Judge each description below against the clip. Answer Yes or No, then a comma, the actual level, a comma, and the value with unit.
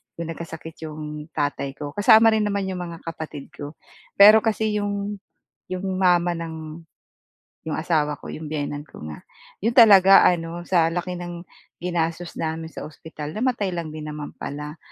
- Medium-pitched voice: Yes, medium, 165 Hz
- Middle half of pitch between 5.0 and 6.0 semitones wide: No, average, 3.7 semitones